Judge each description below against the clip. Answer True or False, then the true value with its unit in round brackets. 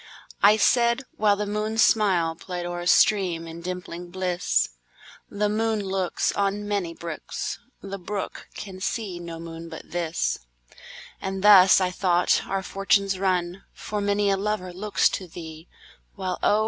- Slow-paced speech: True (125 wpm)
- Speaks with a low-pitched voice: False (190 Hz)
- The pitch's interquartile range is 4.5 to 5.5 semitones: False (2.9 semitones)